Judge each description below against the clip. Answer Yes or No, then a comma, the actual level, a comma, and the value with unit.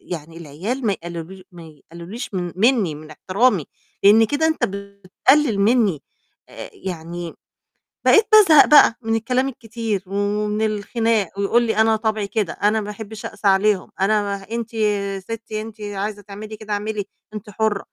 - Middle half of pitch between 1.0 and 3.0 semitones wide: Yes, narrow, 2.6 semitones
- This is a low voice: No, high, 210 Hz